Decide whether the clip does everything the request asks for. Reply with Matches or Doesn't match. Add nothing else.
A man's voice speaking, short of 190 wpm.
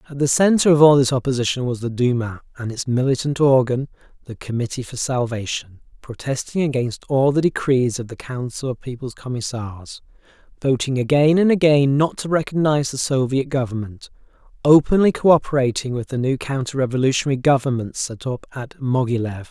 Matches